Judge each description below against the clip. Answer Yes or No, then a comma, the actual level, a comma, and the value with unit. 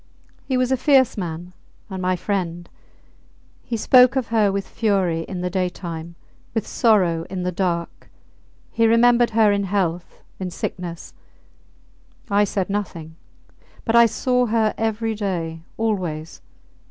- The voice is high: Yes, high, 195 Hz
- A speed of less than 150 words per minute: Yes, average, 140 wpm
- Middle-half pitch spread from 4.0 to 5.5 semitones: Yes, average, 4.3 semitones